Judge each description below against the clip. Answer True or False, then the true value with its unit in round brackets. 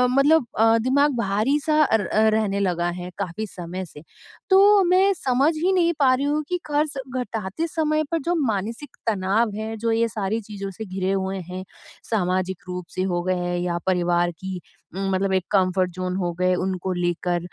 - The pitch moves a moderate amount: False (6.6 semitones)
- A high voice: True (200 Hz)